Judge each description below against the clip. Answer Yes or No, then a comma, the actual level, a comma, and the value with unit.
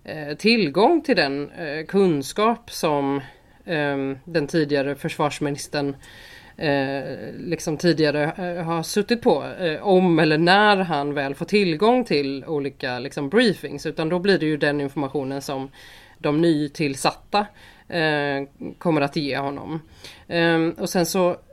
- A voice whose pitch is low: No, medium, 155 Hz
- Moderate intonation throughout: Yes, average, 3.8 semitones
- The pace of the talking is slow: Yes, slow, 115 wpm